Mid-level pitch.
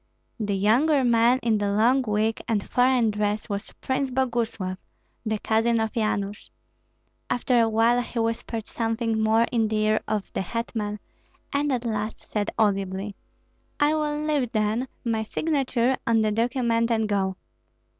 No: high, 225 Hz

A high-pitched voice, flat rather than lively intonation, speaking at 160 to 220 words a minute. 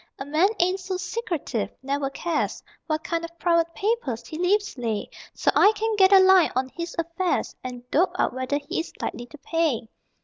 No: very high, 335 Hz; wide, 5.5 semitones; average, 190 wpm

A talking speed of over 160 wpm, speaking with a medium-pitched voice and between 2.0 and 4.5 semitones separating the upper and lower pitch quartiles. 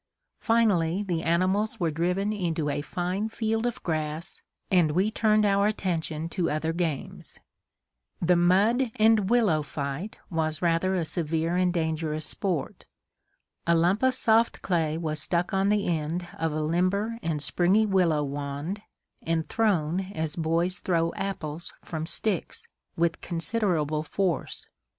No: average, 140 wpm; medium, 175 Hz; average, 3.8 semitones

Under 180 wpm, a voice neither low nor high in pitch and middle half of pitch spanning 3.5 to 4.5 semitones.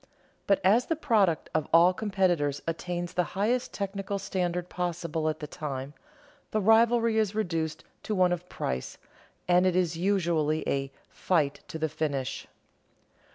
Yes: average, 150 wpm; medium, 175 Hz; average, 4.0 semitones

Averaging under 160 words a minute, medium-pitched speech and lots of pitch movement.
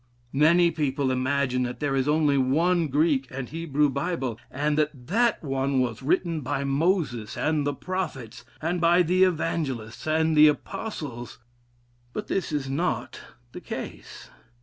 No: average, 150 wpm; medium, 145 Hz; average, 3.9 semitones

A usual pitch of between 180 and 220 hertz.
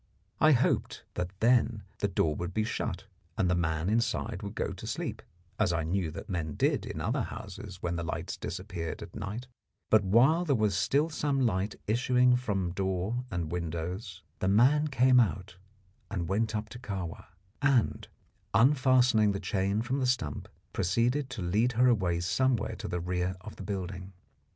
No: low, 105 Hz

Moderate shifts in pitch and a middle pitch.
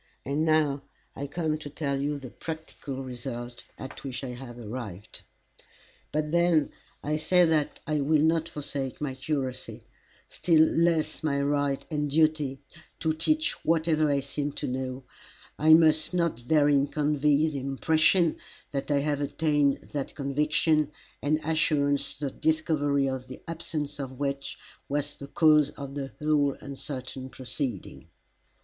No: narrow, 2.2 semitones; medium, 145 Hz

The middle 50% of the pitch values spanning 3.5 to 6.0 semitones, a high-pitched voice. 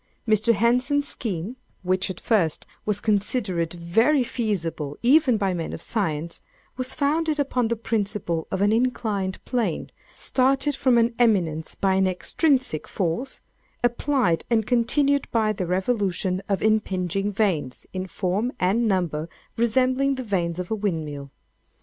Yes: average, 5.3 semitones; high, 210 Hz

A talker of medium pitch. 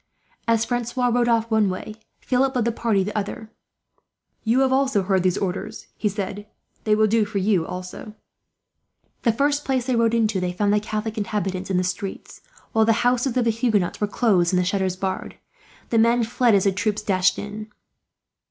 No: high, 215 Hz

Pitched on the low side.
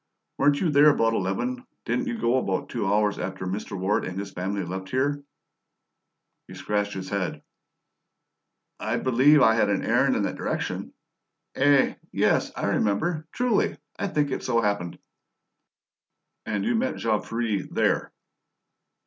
Yes: low, 110 Hz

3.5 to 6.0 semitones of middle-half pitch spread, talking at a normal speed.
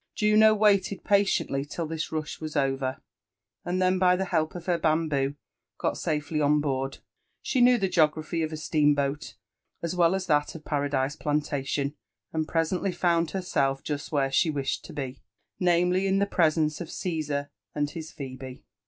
Yes: average, 3.8 semitones; average, 170 wpm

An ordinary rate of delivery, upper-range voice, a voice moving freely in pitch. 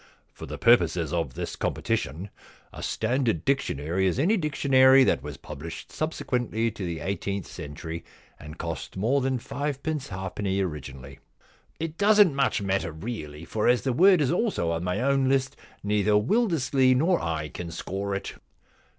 No: average, 165 wpm; low, 105 Hz; wide, 8.4 semitones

